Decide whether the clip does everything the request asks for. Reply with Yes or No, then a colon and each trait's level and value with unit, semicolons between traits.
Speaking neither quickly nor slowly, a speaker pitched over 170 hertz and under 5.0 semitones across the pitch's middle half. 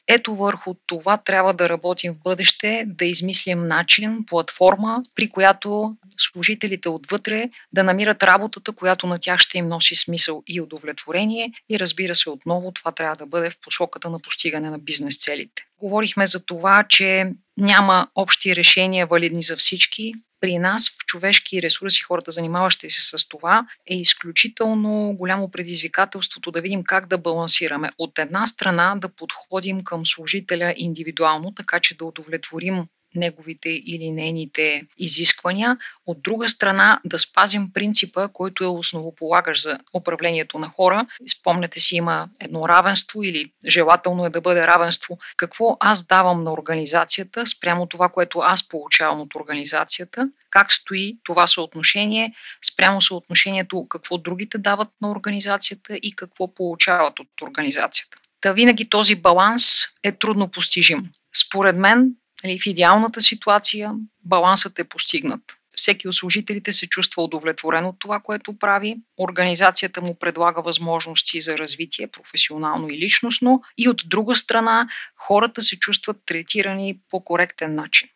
Yes: average, 140 wpm; medium, 185 Hz; average, 3.4 semitones